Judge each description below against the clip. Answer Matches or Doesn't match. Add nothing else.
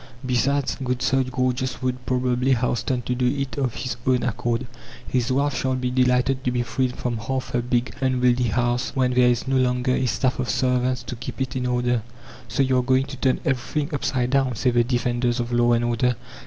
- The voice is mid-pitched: Doesn't match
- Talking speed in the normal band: Doesn't match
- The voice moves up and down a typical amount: Doesn't match